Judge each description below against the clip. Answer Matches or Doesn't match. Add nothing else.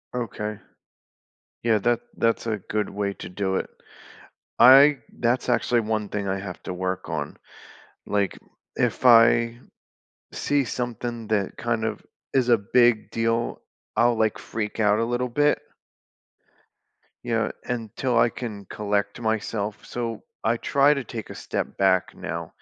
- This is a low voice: Matches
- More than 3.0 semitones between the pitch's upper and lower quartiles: Doesn't match